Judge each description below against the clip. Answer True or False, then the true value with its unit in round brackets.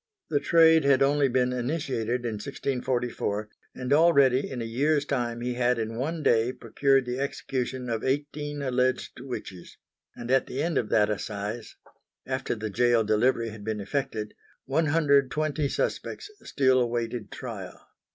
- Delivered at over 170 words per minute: False (160 wpm)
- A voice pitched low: True (125 Hz)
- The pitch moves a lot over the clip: False (3.3 semitones)